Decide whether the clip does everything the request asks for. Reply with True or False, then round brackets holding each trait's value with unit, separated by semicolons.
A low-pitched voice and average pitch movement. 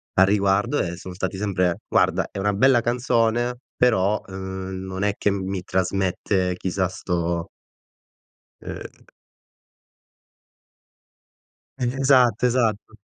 True (95 Hz; 3.7 semitones)